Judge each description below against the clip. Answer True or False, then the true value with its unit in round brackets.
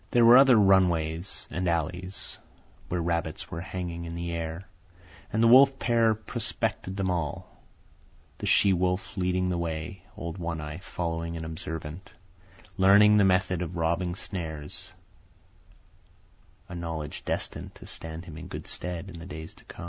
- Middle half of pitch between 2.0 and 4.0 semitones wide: True (2.6 semitones)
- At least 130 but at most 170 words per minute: True (155 wpm)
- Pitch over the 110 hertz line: False (85 Hz)